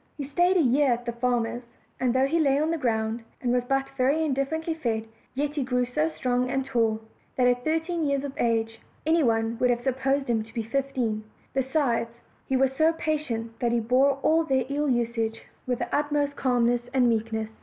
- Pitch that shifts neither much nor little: Yes, average, 3.3 semitones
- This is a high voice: Yes, very high, 255 Hz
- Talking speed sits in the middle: No, fast, 210 wpm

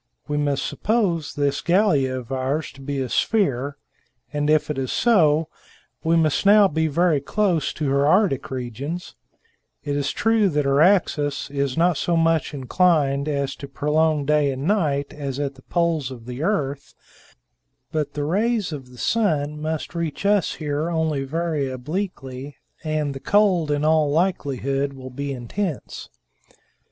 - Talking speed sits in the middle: Yes, average, 160 wpm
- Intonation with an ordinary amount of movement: Yes, average, 3.4 semitones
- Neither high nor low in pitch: Yes, medium, 150 Hz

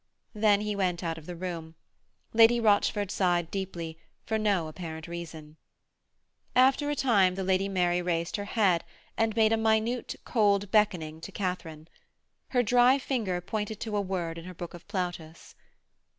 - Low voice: No, high, 190 Hz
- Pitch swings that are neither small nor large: Yes, average, 4.0 semitones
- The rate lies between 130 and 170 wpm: Yes, average, 165 wpm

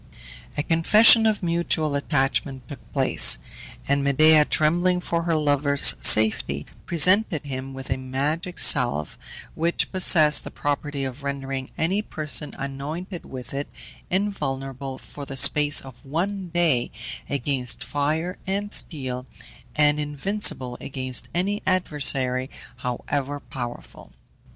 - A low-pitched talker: No, medium, 145 Hz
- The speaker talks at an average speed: No, slow, 120 wpm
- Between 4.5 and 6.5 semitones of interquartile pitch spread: No, average, 4.1 semitones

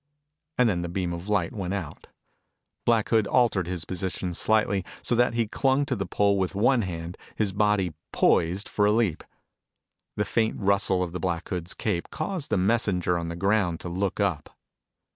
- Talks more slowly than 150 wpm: No, average, 185 wpm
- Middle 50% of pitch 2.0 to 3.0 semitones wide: No, average, 3.6 semitones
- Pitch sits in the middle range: No, very low, 95 Hz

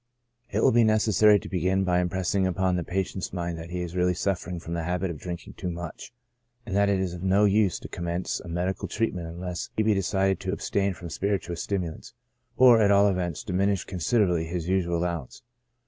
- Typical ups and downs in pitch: No, narrow, 2.3 semitones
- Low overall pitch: Yes, very low, 90 Hz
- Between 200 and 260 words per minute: Yes, fast, 205 wpm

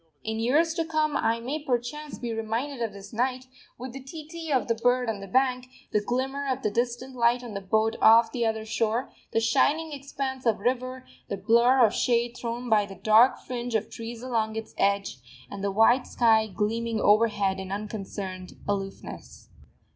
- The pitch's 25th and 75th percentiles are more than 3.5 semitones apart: No, average, 2.9 semitones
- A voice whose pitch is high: Yes, high, 235 Hz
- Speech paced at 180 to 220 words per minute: Yes, average, 190 wpm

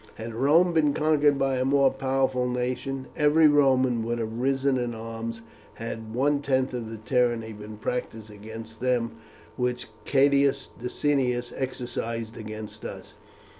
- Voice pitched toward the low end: Yes, low, 125 Hz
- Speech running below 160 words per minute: Yes, average, 140 wpm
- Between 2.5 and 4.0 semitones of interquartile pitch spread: Yes, average, 3.1 semitones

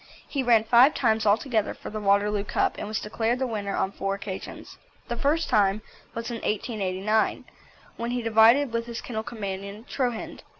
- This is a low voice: No, high, 220 Hz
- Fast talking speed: No, average, 175 wpm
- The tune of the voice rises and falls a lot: No, average, 2.7 semitones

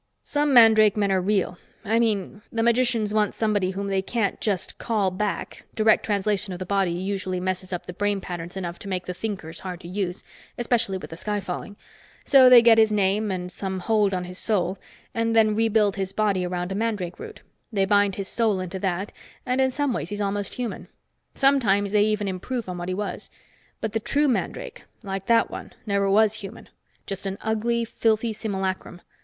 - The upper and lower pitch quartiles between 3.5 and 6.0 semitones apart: No, average, 2.8 semitones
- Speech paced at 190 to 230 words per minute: Yes, average, 200 wpm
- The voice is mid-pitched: No, high, 205 Hz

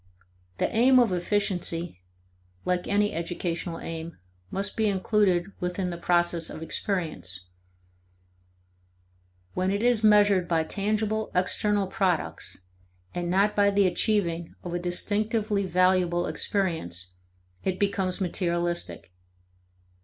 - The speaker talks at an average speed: No, slow, 110 wpm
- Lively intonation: No, average, 2.9 semitones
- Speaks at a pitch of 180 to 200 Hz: Yes, medium, 185 Hz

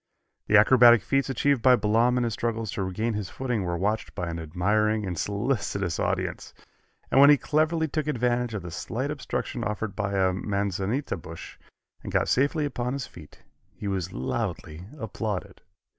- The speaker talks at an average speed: Yes, average, 175 wpm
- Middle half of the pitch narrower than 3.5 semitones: No, average, 4.6 semitones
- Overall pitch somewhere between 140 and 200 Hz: No, low, 110 Hz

